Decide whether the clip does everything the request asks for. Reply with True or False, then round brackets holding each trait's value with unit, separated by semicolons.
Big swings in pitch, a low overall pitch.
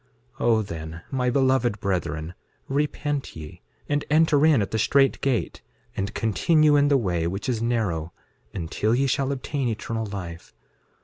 True (6.2 semitones; 115 Hz)